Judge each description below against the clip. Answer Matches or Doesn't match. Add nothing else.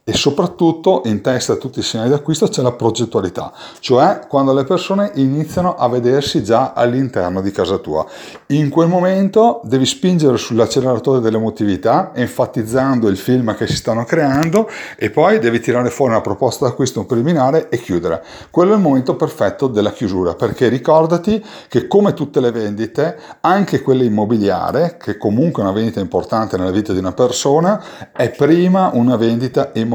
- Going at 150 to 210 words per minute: Matches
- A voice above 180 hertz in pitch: Doesn't match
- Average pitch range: Doesn't match